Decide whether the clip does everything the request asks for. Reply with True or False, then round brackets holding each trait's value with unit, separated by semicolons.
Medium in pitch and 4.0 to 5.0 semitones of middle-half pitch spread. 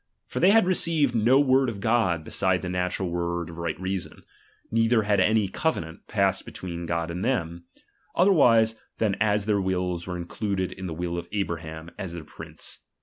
False (95 Hz; 4.6 semitones)